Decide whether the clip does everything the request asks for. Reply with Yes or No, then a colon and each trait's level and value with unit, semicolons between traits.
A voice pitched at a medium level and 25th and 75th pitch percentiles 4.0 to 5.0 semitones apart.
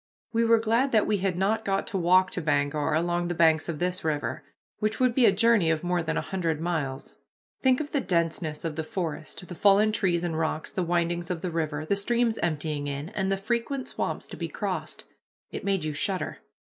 Yes: medium, 175 Hz; average, 4.3 semitones